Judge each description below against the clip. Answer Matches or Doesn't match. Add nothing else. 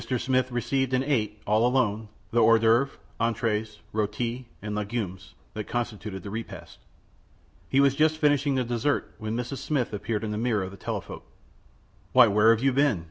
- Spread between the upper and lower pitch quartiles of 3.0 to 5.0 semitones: Matches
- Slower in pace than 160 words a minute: Doesn't match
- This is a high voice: Doesn't match